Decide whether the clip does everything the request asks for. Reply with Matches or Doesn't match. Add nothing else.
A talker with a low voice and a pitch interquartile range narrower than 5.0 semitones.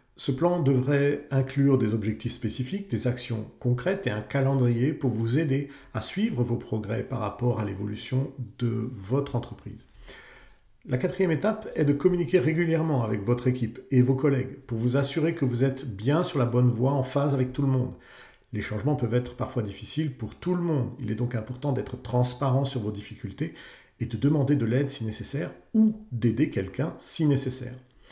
Matches